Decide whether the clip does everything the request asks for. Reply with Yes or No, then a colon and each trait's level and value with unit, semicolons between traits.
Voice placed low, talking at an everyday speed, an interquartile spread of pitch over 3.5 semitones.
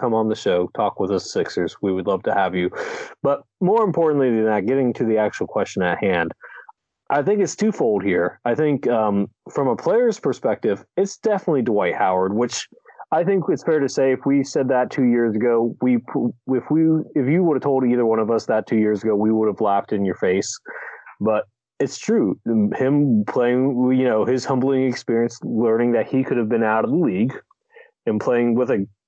No: low, 125 Hz; fast, 215 wpm; average, 4.2 semitones